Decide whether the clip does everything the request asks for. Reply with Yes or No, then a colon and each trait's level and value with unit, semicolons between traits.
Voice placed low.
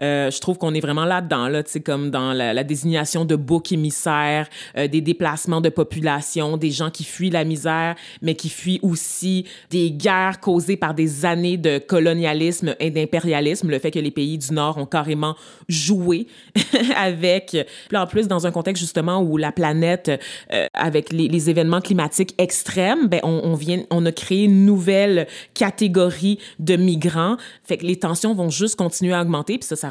No: medium, 170 Hz